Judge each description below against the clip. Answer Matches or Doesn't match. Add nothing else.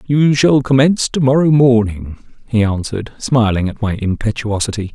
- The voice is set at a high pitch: Doesn't match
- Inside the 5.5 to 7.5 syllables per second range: Doesn't match